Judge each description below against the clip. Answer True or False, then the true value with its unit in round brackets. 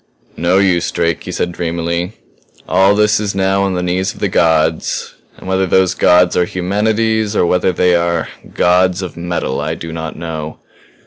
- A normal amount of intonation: False (2.1 semitones)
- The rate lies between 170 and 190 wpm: True (180 wpm)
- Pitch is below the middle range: True (90 Hz)